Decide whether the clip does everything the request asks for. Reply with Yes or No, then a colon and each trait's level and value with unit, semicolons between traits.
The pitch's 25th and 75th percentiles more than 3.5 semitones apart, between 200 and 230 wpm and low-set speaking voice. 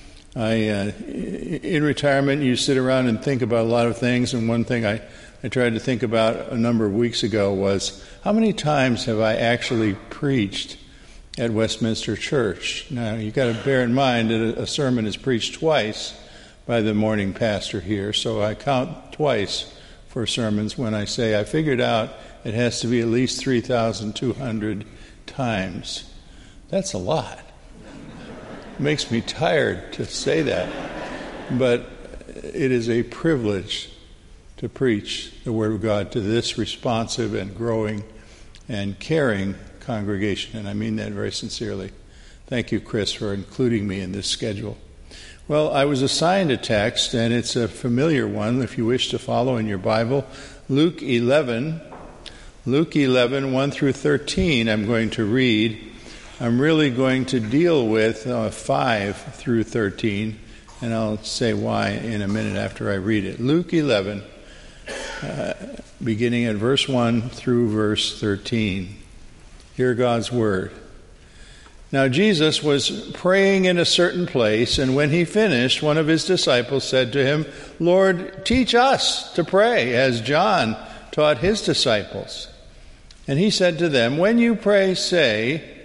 No: average, 4.1 semitones; average, 155 wpm; low, 115 Hz